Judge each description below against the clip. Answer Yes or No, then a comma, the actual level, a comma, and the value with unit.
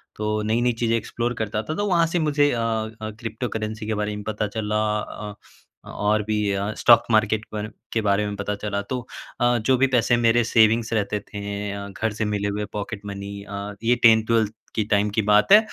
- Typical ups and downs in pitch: No, narrow, 2.0 semitones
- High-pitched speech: No, low, 110 Hz